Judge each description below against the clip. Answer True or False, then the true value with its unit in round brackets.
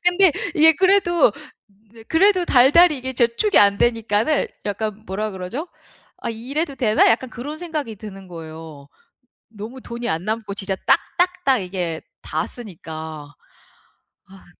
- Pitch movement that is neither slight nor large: False (7.7 semitones)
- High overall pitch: True (230 Hz)